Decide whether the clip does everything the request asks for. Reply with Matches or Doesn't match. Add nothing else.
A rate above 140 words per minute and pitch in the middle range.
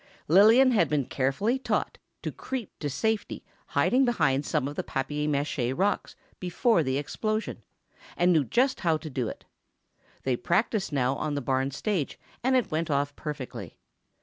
Matches